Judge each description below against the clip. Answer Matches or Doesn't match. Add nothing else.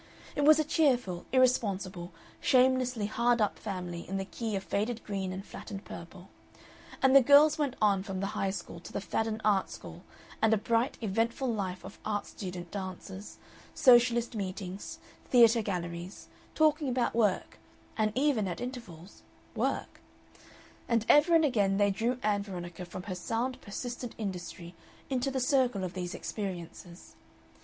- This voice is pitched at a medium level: Doesn't match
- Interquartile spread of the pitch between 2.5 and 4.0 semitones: Doesn't match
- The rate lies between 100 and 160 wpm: Matches